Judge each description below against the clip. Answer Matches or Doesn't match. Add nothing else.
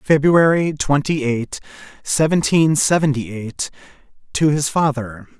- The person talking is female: Doesn't match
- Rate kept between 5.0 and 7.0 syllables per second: Doesn't match